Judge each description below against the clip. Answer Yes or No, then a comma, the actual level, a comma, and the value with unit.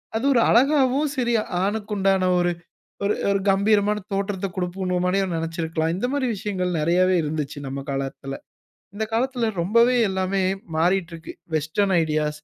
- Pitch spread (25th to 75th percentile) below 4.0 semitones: No, average, 4.4 semitones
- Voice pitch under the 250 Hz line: Yes, high, 190 Hz